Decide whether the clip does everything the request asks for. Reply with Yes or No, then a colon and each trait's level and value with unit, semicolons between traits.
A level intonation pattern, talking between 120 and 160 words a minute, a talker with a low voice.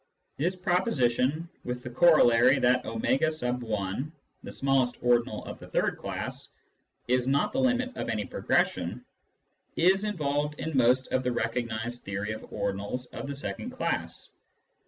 No: average, 4.7 semitones; average, 145 wpm; low, 130 Hz